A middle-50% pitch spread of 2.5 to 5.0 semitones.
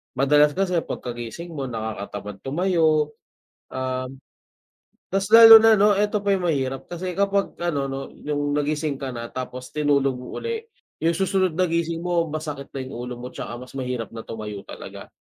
No: wide, 5.6 semitones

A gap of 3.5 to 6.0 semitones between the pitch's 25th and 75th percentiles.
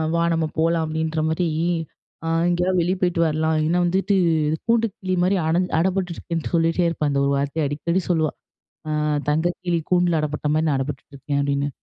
No: narrow, 2.6 semitones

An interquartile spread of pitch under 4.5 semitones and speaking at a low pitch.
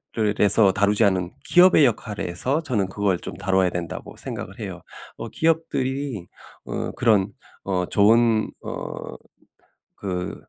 No: average, 5.0 semitones; low, 105 Hz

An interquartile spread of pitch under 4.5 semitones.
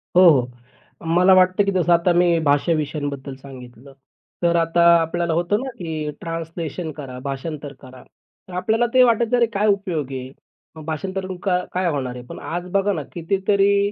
No: average, 4.8 semitones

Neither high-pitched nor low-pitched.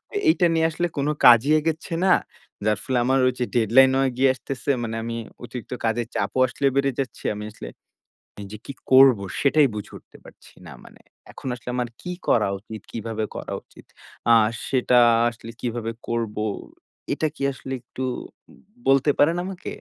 No: low, 125 Hz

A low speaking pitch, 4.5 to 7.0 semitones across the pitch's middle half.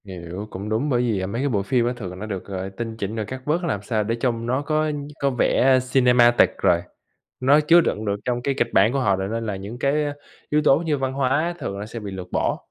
Yes: low, 120 Hz; average, 5.1 semitones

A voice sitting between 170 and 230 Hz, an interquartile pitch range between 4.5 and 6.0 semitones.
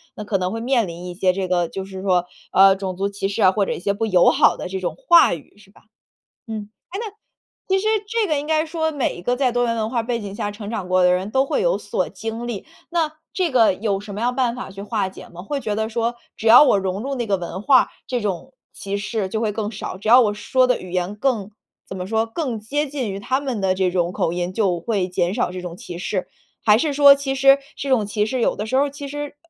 Yes: high, 215 Hz; average, 5.2 semitones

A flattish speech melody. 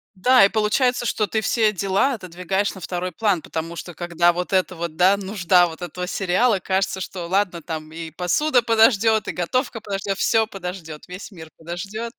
No: average, 3.7 semitones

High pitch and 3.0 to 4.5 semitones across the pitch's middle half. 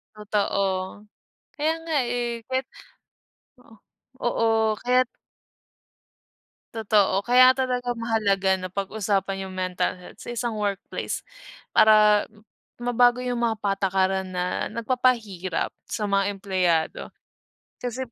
Yes: high, 210 Hz; average, 3.9 semitones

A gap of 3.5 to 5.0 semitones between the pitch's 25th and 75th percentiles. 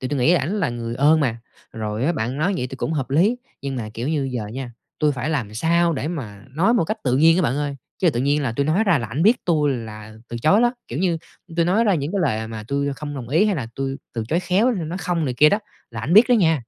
No: wide, 5.5 semitones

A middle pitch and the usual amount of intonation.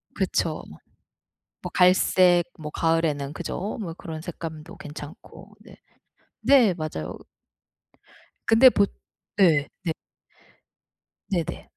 Yes: medium, 165 Hz; average, 3.3 semitones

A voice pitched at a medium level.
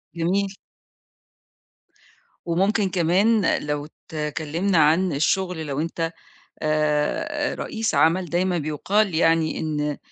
Yes: medium, 165 Hz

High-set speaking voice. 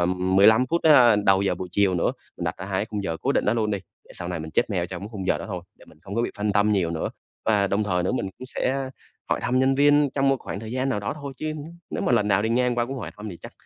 No: low, 105 Hz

